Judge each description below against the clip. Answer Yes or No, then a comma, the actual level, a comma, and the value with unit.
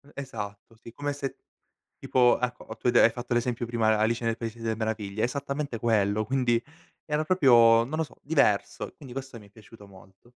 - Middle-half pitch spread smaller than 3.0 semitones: No, average, 3.3 semitones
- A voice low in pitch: Yes, low, 115 Hz